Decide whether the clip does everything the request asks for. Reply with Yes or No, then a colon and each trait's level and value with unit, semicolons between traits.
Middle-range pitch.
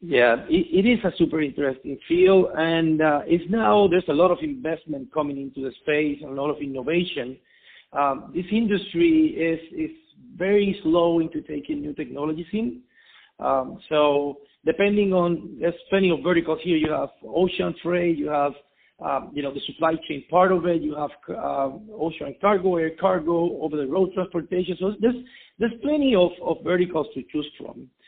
Yes: medium, 170 Hz